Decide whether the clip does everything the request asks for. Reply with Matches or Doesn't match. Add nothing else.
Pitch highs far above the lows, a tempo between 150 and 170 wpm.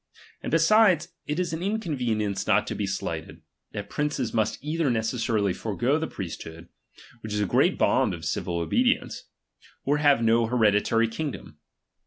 Matches